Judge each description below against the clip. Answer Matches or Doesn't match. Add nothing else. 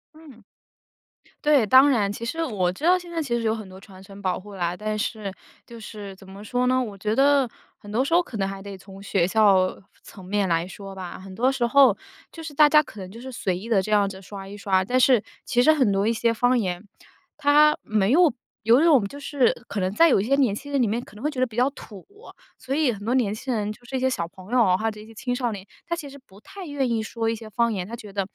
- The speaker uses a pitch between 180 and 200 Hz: Doesn't match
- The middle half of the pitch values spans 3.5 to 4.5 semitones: Doesn't match